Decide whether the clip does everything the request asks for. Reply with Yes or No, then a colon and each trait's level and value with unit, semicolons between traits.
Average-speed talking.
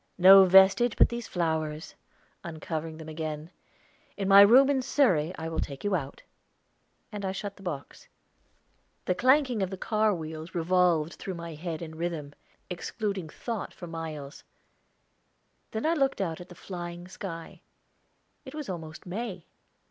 Yes: average, 155 wpm